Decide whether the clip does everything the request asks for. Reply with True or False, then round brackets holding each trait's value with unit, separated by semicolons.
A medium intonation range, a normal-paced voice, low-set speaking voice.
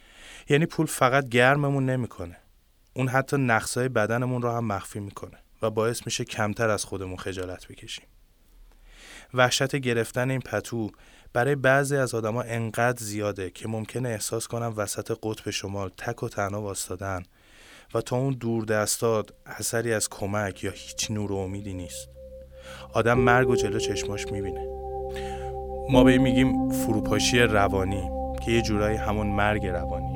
True (4.4 semitones; 145 wpm; 105 Hz)